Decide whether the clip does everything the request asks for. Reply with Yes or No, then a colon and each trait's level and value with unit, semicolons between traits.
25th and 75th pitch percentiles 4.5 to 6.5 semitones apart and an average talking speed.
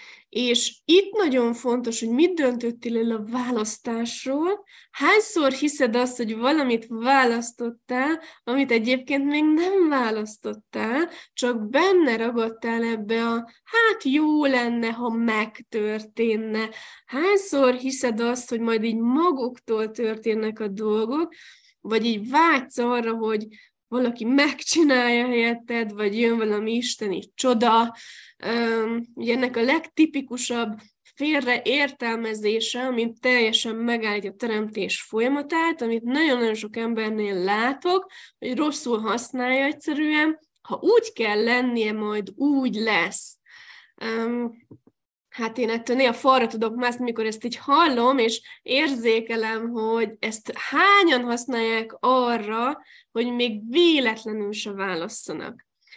No: average, 3.5 semitones; average, 115 wpm